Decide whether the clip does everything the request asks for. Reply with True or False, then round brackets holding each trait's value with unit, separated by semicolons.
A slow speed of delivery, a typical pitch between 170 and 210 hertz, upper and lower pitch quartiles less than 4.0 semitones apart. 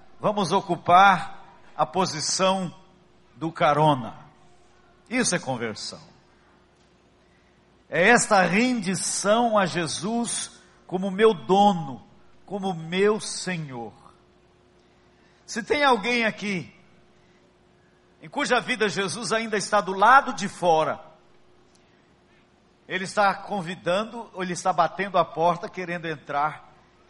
True (100 wpm; 190 Hz; 3.5 semitones)